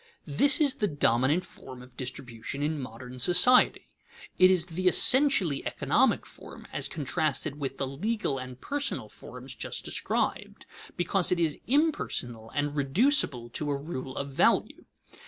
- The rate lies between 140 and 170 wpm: Yes, average, 150 wpm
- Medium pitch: Yes, medium, 145 Hz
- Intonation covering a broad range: Yes, wide, 6.0 semitones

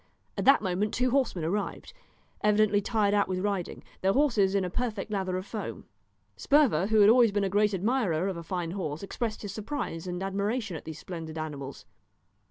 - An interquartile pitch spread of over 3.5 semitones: No, average, 3.0 semitones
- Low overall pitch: No, high, 200 Hz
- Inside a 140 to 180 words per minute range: No, average, 190 wpm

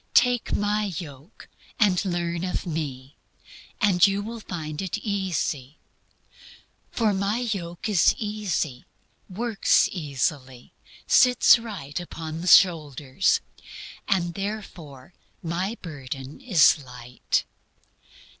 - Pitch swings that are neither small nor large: No, wide, 5.7 semitones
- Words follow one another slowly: Yes, slow, 100 wpm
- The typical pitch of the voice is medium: Yes, medium, 175 Hz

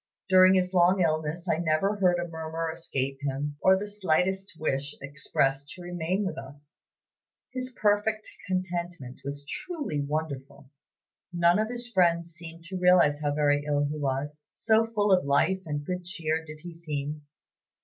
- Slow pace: No, average, 160 wpm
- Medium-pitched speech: Yes, medium, 165 Hz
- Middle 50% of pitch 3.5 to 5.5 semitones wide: Yes, average, 4.2 semitones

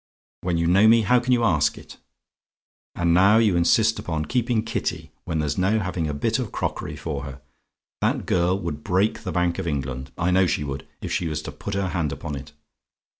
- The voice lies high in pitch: No, very low, 85 Hz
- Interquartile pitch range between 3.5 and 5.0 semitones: Yes, average, 4.5 semitones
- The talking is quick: Yes, fast, 215 wpm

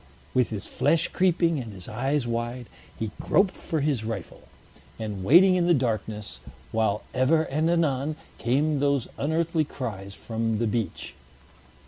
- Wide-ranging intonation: Yes, wide, 5.9 semitones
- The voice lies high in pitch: No, low, 130 Hz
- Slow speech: No, average, 145 wpm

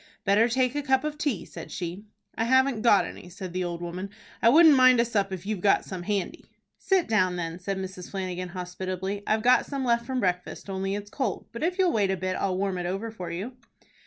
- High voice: Yes, high, 200 Hz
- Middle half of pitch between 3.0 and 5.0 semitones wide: Yes, average, 4.7 semitones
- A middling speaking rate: No, fast, 230 wpm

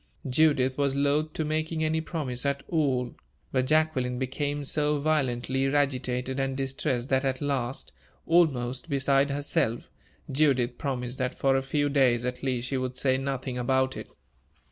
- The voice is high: No, low, 135 Hz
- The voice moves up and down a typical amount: No, narrow, 2.2 semitones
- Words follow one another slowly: No, average, 155 wpm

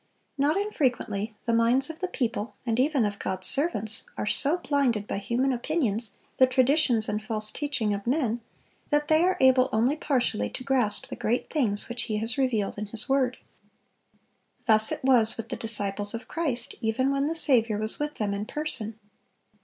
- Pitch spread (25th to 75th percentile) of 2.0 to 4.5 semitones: Yes, average, 4.2 semitones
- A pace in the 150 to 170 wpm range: No, average, 185 wpm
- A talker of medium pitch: No, high, 240 Hz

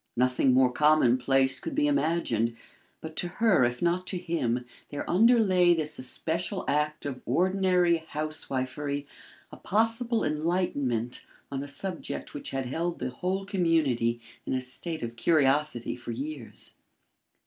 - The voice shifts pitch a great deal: Yes, wide, 5.7 semitones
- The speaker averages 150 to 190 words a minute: No, slow, 135 wpm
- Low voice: No, medium, 150 Hz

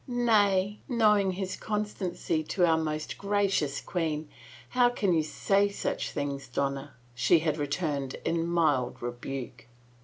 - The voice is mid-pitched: Yes, medium, 165 Hz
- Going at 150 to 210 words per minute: No, average, 140 wpm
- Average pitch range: No, wide, 5.8 semitones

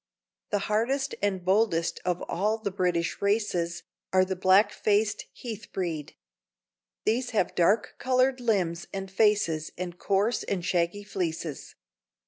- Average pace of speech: No, slow, 130 wpm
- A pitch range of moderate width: Yes, average, 3.4 semitones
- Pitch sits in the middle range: No, high, 195 Hz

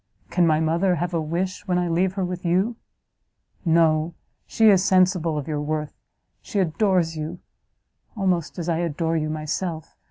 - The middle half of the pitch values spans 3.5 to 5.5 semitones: No, narrow, 2.6 semitones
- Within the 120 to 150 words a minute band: No, average, 165 wpm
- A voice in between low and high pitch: Yes, medium, 170 Hz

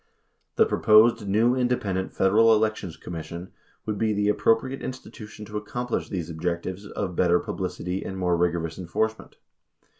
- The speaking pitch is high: No, low, 100 Hz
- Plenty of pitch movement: No, average, 3.8 semitones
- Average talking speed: Yes, average, 145 wpm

